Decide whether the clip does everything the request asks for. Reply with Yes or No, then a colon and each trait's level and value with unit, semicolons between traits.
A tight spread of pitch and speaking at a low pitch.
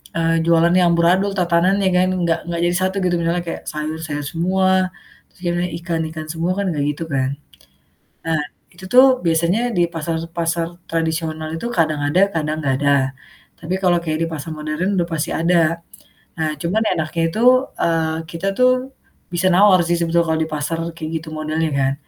No: narrow, 1.8 semitones; medium, 165 Hz